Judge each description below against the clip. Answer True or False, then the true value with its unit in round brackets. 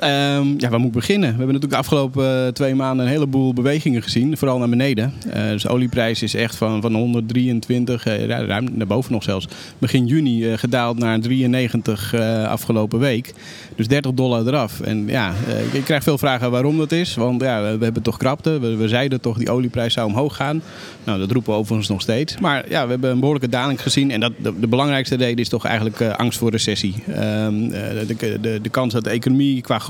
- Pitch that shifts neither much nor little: True (3.0 semitones)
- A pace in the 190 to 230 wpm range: True (195 wpm)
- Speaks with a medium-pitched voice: False (120 Hz)